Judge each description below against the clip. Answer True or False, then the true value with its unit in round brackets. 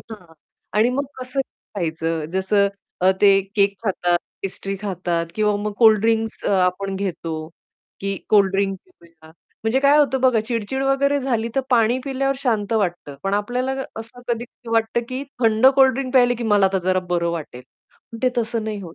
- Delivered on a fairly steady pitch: False (4.3 semitones)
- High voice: True (215 Hz)